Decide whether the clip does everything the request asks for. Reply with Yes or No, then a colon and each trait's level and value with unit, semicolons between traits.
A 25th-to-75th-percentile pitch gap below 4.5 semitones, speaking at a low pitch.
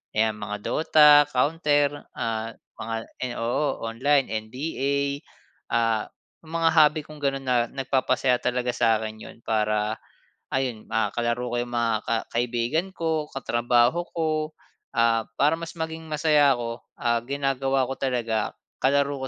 Yes: average, 4.1 semitones; low, 130 Hz